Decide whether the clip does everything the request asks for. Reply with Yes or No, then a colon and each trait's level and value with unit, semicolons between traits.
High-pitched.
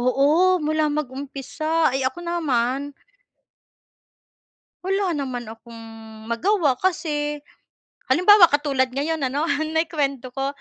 Yes: very high, 285 Hz